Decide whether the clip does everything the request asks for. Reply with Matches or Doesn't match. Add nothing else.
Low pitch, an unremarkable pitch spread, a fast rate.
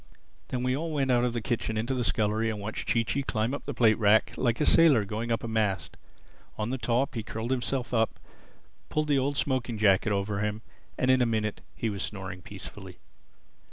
Matches